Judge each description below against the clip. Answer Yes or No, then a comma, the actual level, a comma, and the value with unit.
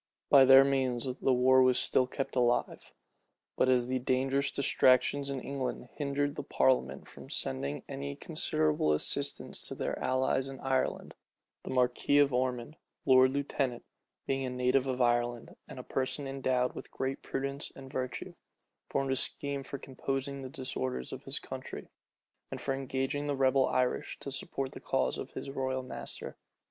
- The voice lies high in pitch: No, low, 130 Hz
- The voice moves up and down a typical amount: No, narrow, 1.3 semitones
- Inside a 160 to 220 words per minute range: Yes, average, 165 wpm